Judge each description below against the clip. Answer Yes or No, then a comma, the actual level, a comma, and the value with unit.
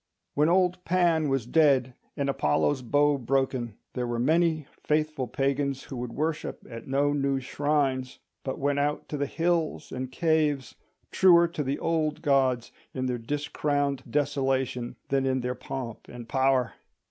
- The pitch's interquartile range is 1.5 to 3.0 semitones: Yes, average, 2.7 semitones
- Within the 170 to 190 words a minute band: No, average, 155 wpm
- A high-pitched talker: No, medium, 140 Hz